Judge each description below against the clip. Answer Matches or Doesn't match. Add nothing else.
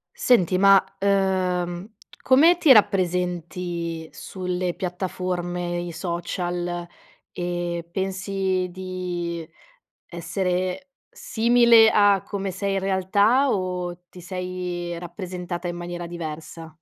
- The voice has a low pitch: Doesn't match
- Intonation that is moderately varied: Doesn't match